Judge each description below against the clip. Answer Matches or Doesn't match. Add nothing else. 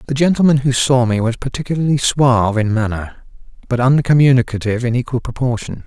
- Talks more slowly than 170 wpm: Matches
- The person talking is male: Matches